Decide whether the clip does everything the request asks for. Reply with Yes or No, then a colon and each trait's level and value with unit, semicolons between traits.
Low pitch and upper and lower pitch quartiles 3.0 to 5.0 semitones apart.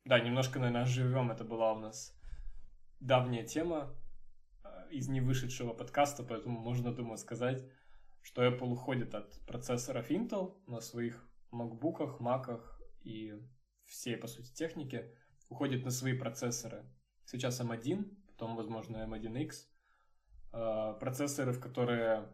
No: low, 120 Hz; narrow, 2.5 semitones